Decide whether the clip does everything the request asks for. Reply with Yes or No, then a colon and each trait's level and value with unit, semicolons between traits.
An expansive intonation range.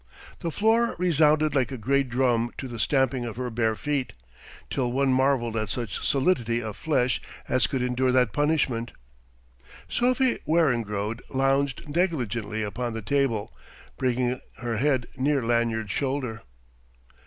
No: average, 3.3 semitones